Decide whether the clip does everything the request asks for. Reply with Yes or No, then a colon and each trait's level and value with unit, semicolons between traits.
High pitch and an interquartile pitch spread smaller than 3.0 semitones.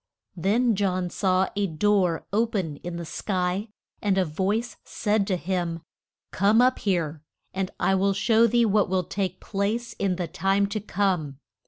Yes: high, 195 Hz; narrow, 2.5 semitones